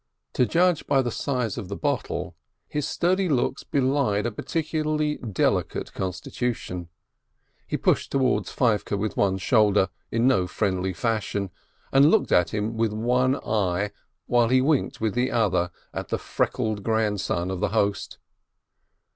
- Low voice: Yes, low, 110 Hz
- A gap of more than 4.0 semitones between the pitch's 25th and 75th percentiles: Yes, average, 4.8 semitones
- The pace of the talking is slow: No, average, 145 wpm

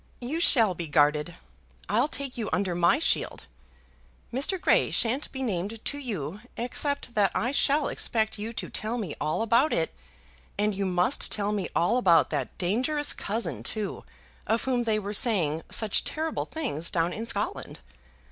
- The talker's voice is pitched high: Yes, high, 220 Hz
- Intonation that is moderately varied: No, wide, 5.8 semitones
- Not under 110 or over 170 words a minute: Yes, average, 165 wpm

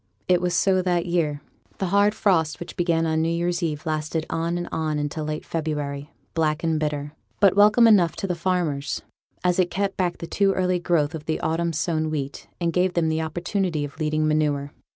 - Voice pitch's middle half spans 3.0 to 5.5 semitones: No, narrow, 2.6 semitones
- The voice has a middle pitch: Yes, medium, 165 Hz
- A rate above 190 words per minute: Yes, average, 200 wpm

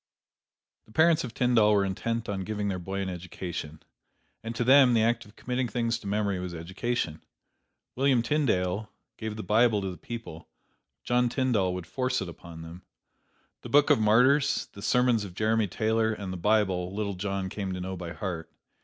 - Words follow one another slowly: No, average, 185 wpm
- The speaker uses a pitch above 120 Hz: No, low, 105 Hz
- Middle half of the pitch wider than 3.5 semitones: Yes, average, 4.3 semitones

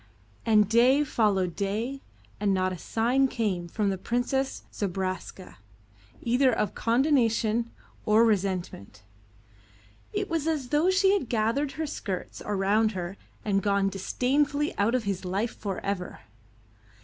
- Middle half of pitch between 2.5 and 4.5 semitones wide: No, average, 4.9 semitones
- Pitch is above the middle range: Yes, high, 220 Hz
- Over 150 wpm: No, slow, 135 wpm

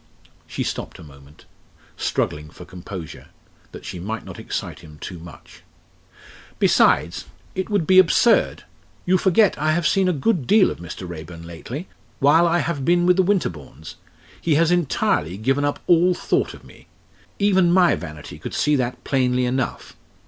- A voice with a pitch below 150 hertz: Yes, medium, 140 Hz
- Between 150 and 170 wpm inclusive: Yes, average, 165 wpm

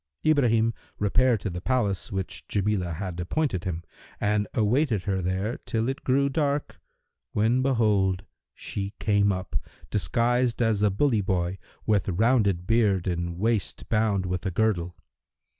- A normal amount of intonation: Yes, average, 3.8 semitones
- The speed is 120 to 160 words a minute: Yes, average, 140 wpm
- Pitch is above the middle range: No, low, 105 Hz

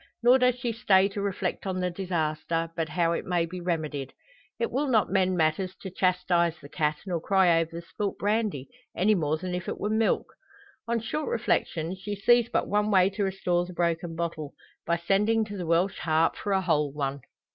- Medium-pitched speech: Yes, medium, 180 Hz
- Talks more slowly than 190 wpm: No, fast, 205 wpm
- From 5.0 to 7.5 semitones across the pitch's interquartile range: No, average, 3.5 semitones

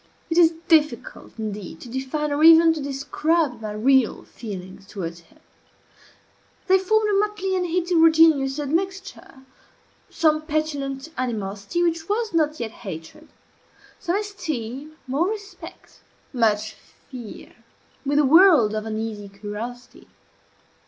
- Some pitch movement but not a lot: No, wide, 7.0 semitones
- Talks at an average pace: No, slow, 120 wpm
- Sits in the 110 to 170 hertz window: No, very high, 285 Hz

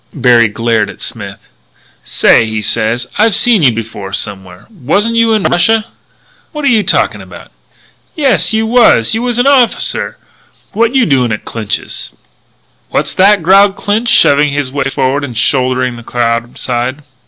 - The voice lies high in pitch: No, medium, 140 Hz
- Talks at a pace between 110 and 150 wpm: No, average, 160 wpm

